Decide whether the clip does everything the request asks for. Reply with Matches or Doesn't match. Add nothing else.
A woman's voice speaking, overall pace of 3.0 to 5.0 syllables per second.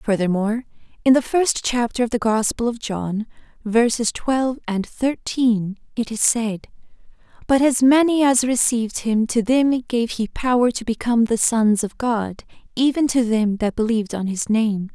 Matches